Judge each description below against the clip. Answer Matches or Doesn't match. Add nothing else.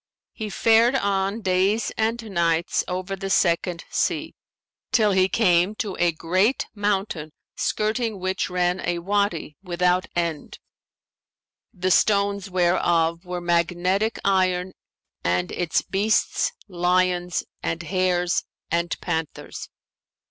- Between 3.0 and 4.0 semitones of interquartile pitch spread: Doesn't match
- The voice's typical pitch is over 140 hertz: Matches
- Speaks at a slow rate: Matches